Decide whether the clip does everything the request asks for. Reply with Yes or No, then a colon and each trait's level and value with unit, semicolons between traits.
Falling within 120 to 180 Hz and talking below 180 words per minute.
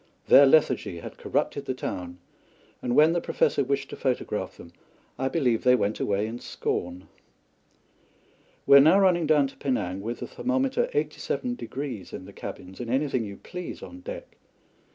Yes: low, 135 Hz; average, 165 wpm